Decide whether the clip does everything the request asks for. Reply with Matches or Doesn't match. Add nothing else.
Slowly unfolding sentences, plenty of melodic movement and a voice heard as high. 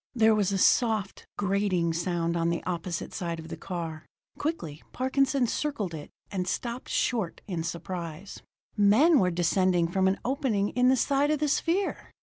Doesn't match